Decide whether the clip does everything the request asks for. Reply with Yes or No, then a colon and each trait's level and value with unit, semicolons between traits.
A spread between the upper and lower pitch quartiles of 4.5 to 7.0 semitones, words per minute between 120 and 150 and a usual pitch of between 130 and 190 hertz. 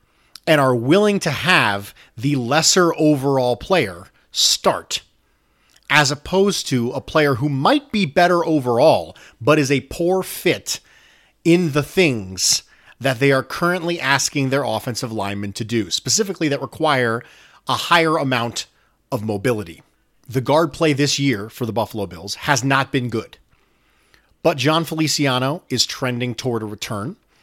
Yes: average, 4.8 semitones; average, 145 wpm; low, 135 Hz